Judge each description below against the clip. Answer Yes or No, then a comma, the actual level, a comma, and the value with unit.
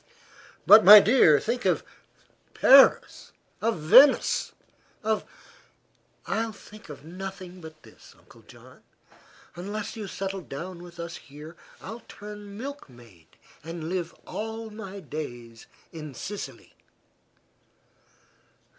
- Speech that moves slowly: Yes, slow, 110 wpm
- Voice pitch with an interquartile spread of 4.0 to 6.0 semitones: Yes, average, 5.3 semitones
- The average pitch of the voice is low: No, high, 190 Hz